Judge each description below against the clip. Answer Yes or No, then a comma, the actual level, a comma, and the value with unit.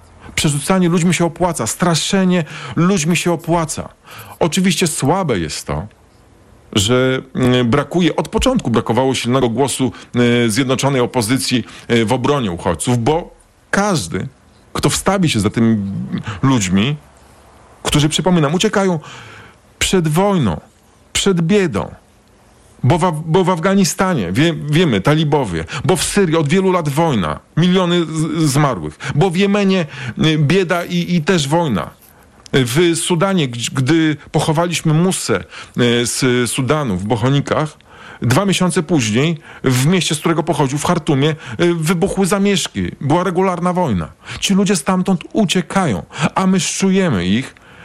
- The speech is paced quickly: No, average, 120 wpm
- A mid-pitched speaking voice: Yes, medium, 160 Hz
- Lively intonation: Yes, wide, 6.5 semitones